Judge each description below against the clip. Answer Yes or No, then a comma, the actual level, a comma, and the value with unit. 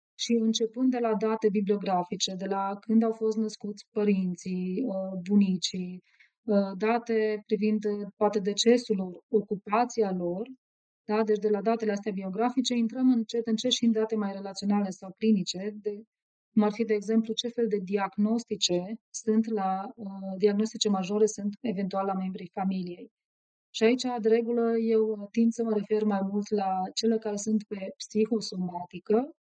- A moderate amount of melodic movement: No, narrow, 2.3 semitones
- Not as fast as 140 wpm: No, average, 150 wpm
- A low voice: No, high, 215 Hz